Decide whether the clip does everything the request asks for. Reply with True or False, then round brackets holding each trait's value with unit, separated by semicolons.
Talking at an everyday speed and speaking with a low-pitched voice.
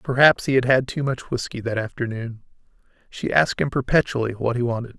True (195 wpm; 125 Hz)